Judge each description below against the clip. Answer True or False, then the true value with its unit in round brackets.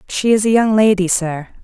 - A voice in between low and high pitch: False (200 Hz)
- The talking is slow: False (220 wpm)